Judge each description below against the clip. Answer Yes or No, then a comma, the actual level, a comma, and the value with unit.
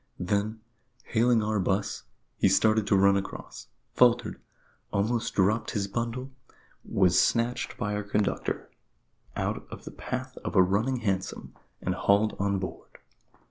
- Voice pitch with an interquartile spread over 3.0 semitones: No, average, 2.7 semitones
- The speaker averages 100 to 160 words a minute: Yes, average, 140 wpm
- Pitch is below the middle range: Yes, low, 105 Hz